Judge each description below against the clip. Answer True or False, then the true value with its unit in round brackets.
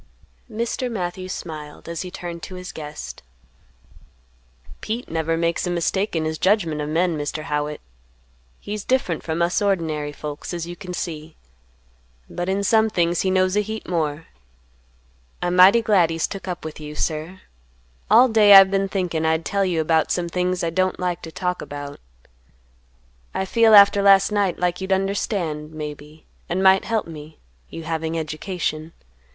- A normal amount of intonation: True (3.4 semitones)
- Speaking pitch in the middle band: True (175 Hz)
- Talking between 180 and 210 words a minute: False (170 wpm)